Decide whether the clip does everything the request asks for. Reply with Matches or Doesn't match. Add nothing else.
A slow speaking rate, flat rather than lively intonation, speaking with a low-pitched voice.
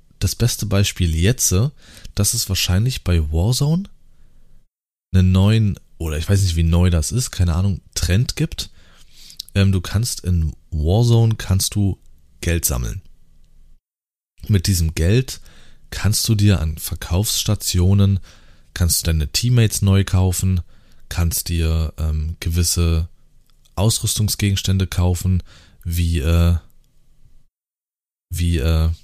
Doesn't match